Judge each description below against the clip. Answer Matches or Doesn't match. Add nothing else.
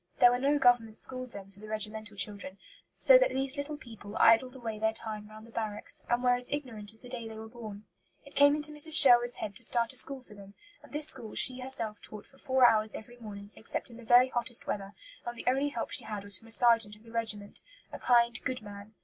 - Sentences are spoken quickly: Matches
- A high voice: Matches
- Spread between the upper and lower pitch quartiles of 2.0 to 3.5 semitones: Matches